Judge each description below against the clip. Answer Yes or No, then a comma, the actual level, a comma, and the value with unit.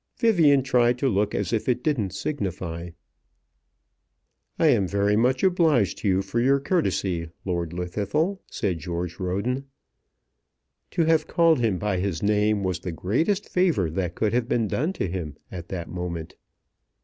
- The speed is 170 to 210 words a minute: No, average, 160 wpm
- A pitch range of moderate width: No, wide, 7.0 semitones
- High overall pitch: No, low, 105 Hz